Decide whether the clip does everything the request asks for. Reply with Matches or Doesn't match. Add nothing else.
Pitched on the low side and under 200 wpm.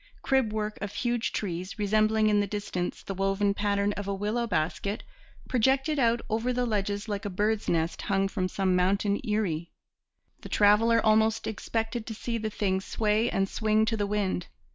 Doesn't match